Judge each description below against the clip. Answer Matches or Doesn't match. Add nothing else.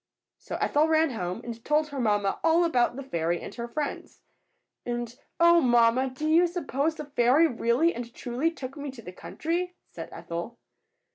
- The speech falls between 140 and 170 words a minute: Doesn't match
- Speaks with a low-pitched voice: Doesn't match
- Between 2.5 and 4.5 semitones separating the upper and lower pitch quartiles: Doesn't match